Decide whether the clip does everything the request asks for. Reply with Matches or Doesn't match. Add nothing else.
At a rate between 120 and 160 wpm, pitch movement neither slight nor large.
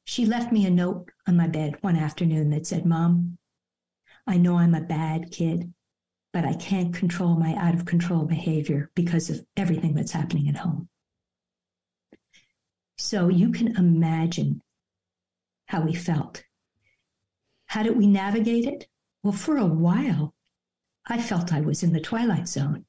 Matches